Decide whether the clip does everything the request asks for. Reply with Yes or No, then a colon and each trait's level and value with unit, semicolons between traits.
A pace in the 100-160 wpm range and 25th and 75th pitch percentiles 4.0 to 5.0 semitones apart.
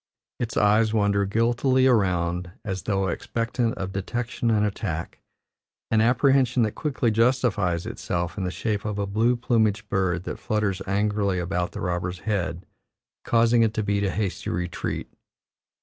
No: average, 150 wpm; average, 3.6 semitones